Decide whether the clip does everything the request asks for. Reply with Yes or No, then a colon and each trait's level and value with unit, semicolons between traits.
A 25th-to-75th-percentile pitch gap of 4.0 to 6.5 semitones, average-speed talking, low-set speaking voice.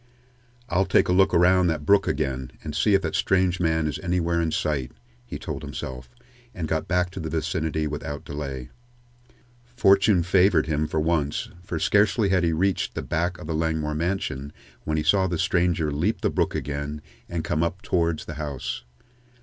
No: average, 3.1 semitones; average, 185 wpm; very low, 80 Hz